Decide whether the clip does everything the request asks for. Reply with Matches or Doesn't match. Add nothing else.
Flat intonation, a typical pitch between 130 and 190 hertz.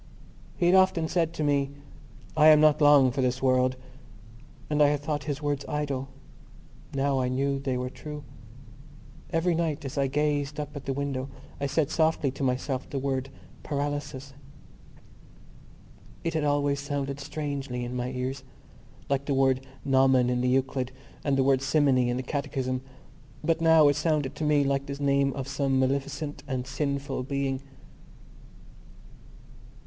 Matches